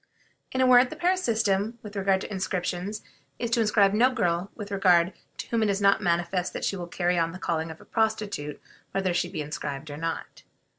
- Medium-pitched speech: No, high, 195 Hz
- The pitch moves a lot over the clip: No, average, 3.9 semitones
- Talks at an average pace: No, fast, 215 wpm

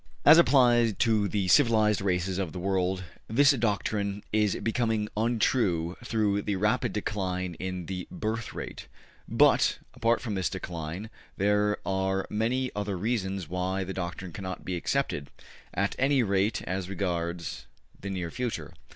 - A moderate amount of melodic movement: Yes, average, 3.3 semitones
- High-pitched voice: No, low, 100 Hz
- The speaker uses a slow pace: No, average, 145 wpm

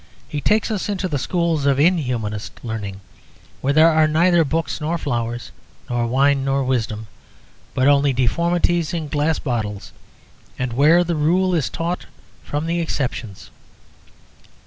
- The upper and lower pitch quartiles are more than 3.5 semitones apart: Yes, average, 5.2 semitones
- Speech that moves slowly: No, average, 145 wpm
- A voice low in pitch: No, medium, 145 Hz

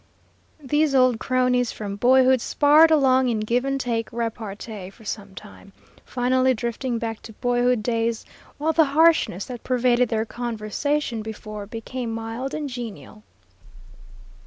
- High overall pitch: Yes, high, 245 Hz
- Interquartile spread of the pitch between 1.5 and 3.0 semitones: Yes, average, 2.7 semitones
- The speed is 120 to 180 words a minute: Yes, slow, 135 wpm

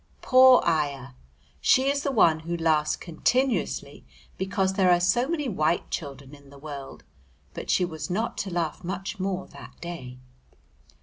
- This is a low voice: No, medium, 175 Hz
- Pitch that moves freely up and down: No, average, 4.4 semitones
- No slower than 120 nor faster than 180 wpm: Yes, average, 160 wpm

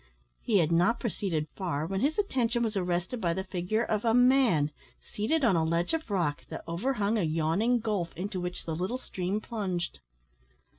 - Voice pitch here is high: Yes, high, 195 Hz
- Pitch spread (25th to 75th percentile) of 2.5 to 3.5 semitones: No, average, 5.1 semitones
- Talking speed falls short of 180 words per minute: No, average, 190 wpm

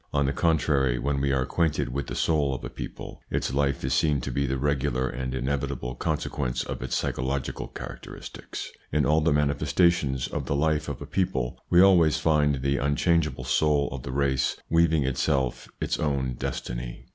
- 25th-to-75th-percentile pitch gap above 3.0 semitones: No, average, 2.7 semitones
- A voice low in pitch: Yes, very low, 70 Hz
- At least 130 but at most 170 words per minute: No, average, 185 wpm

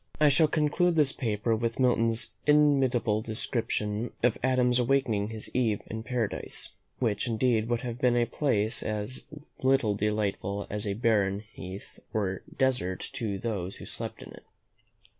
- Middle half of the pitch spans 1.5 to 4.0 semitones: Yes, average, 3.4 semitones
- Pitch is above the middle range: No, low, 115 Hz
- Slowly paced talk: No, average, 150 wpm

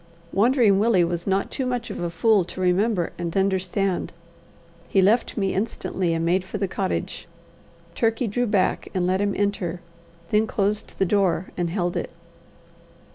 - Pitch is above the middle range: Yes, high, 195 Hz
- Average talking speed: Yes, average, 160 wpm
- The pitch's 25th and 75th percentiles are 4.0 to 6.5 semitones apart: No, average, 2.8 semitones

